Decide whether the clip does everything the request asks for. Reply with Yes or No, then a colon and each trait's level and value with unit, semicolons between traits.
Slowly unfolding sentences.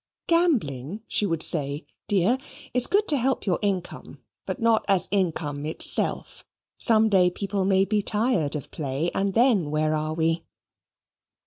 No: average, 155 wpm